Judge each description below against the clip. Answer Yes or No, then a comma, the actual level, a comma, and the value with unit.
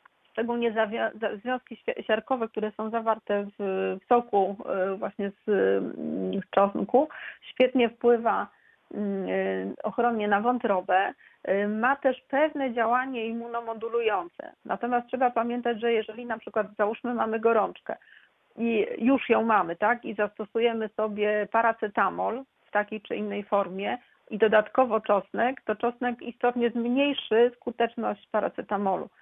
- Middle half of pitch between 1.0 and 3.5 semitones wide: Yes, narrow, 2.6 semitones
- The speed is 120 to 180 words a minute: No, slow, 110 wpm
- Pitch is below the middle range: No, high, 225 Hz